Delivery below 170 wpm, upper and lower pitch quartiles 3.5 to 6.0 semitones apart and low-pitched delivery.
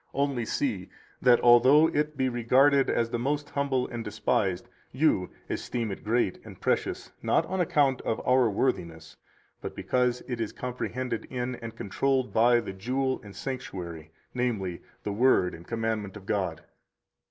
Yes: average, 155 wpm; average, 4.3 semitones; low, 120 Hz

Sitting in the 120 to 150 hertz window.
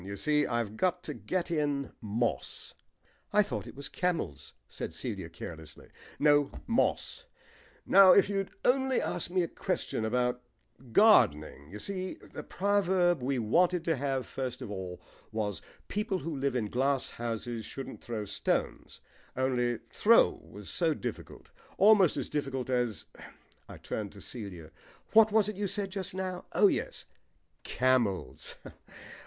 Yes: medium, 140 Hz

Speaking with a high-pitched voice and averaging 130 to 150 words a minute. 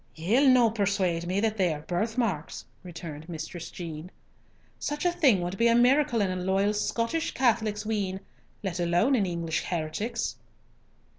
No: high, 195 Hz; average, 160 wpm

